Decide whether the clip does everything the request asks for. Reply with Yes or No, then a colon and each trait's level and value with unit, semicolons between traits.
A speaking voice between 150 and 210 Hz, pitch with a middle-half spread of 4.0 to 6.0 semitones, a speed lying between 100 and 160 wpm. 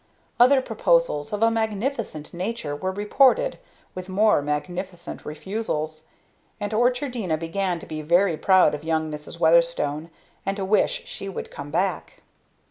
Yes: medium, 185 Hz; average, 5.2 semitones; average, 140 wpm